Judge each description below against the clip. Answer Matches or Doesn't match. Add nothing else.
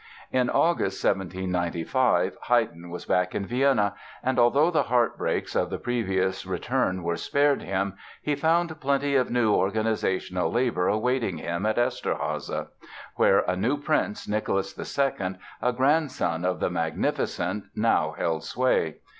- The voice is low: Matches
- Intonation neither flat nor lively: Doesn't match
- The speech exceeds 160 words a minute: Doesn't match